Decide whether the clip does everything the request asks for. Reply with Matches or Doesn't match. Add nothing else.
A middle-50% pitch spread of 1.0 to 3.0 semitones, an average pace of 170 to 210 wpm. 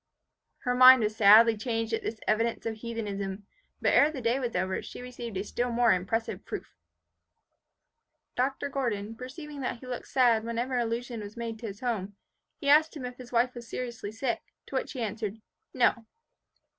Matches